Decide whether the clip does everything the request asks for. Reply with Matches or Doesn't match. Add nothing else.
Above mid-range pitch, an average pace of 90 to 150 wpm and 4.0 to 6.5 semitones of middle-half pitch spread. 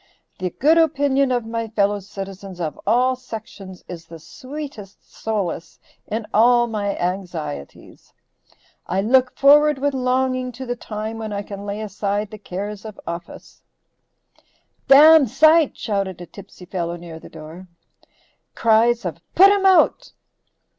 Matches